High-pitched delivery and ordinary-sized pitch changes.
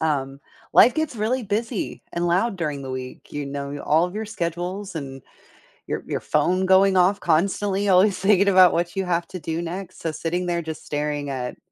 No: medium, 175 Hz; average, 4.3 semitones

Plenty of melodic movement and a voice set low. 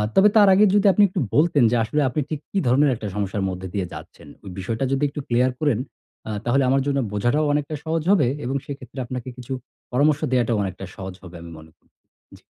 Yes: wide, 5.8 semitones; low, 130 Hz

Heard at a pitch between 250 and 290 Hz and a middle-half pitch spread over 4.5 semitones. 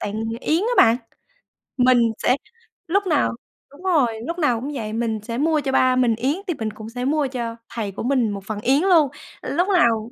Yes: very high, 255 Hz; average, 5.0 semitones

